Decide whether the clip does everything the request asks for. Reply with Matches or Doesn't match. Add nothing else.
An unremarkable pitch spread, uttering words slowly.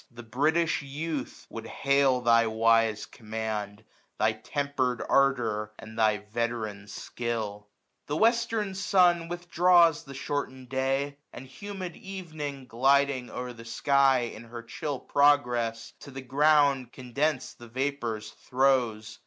Matches